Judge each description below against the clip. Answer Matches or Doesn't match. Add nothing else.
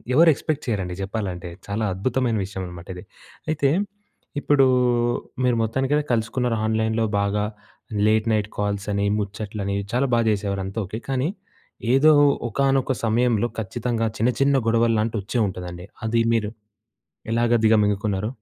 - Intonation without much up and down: Doesn't match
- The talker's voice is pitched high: Doesn't match